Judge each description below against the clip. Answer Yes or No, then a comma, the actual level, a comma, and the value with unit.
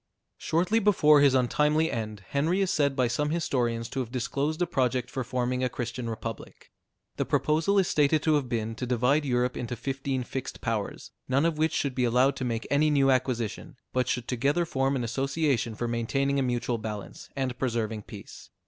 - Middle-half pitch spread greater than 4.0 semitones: No, average, 3.4 semitones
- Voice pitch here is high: No, low, 130 Hz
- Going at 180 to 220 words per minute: Yes, average, 195 wpm